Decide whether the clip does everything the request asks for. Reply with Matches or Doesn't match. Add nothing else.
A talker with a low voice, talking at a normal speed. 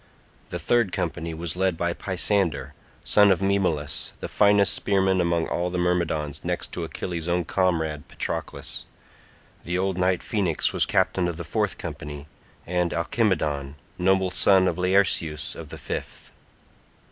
Matches